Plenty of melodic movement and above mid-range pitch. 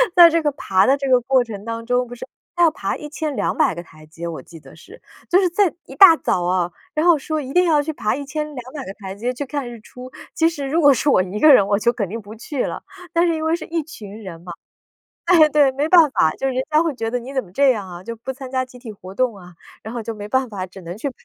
Yes: wide, 6.6 semitones; very high, 255 Hz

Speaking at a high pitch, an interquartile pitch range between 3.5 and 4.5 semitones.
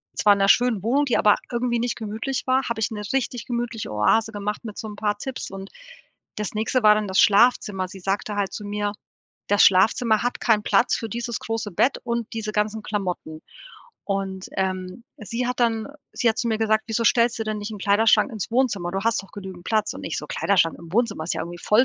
No: high, 215 Hz; average, 2.8 semitones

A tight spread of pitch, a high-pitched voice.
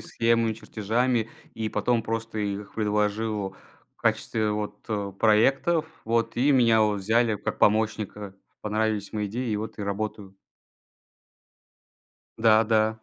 No: narrow, 1.5 semitones; low, 110 Hz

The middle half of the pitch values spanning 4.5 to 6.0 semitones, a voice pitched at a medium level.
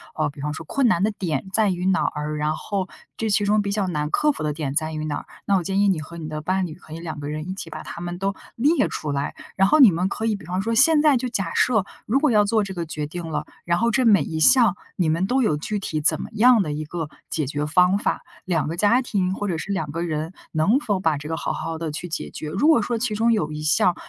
Yes: average, 5.2 semitones; medium, 180 Hz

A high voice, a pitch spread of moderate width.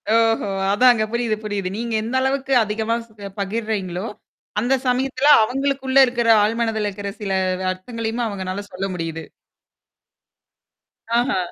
Yes: high, 225 Hz; average, 3.4 semitones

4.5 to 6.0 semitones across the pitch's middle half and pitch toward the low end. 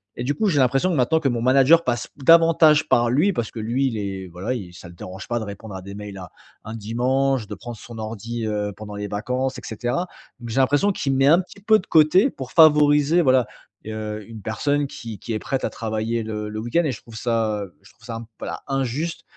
Yes: average, 4.8 semitones; low, 120 Hz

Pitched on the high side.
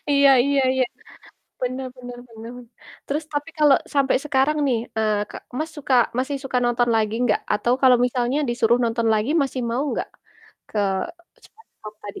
Yes: very high, 255 Hz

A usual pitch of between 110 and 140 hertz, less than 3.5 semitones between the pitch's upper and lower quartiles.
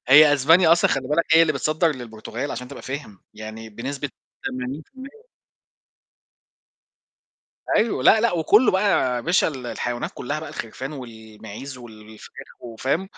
No: low, 135 Hz; average, 5.3 semitones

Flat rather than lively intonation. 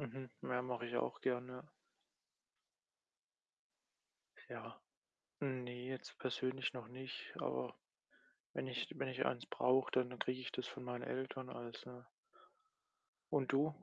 Yes: narrow, 1.1 semitones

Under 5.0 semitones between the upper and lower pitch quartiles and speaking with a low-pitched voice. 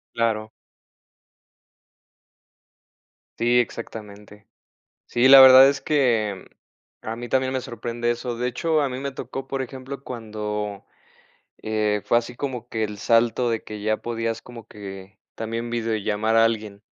Yes: average, 2.8 semitones; low, 115 Hz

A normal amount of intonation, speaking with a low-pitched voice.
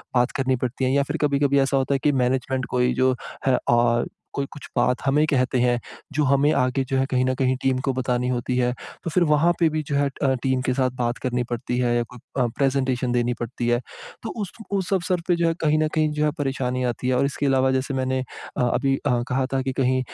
No: narrow, 2.1 semitones; low, 130 Hz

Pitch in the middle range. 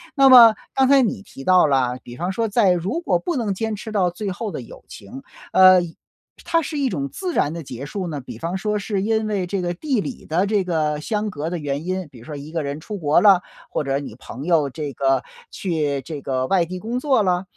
Yes: medium, 180 Hz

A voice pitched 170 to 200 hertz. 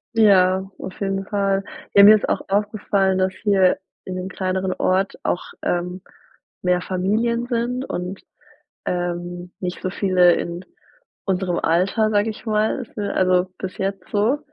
Yes: high, 190 Hz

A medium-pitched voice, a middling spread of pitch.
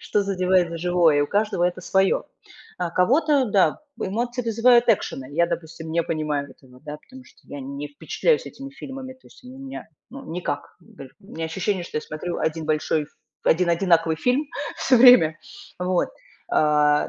No: medium, 180 Hz; wide, 7.1 semitones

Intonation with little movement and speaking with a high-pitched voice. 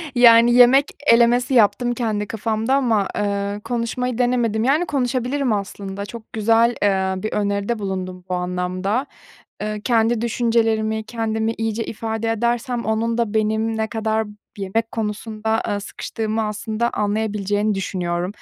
Yes: narrow, 2.3 semitones; high, 220 Hz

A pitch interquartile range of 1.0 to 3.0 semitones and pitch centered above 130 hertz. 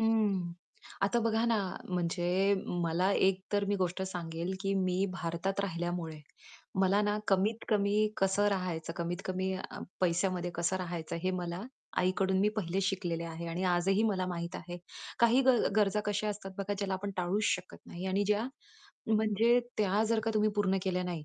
Yes: average, 2.7 semitones; high, 190 Hz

